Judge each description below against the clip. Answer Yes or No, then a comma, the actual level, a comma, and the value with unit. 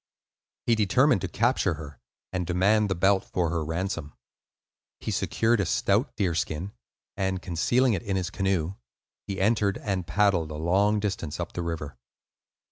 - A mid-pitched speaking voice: No, very low, 95 Hz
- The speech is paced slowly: No, average, 155 wpm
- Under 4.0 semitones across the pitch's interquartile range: Yes, average, 3.5 semitones